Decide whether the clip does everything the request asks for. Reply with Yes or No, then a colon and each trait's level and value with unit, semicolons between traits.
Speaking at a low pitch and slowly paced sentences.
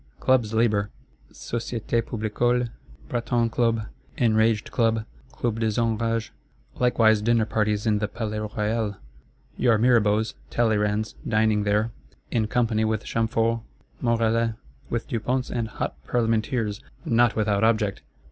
Yes: low, 115 Hz; slow, 120 wpm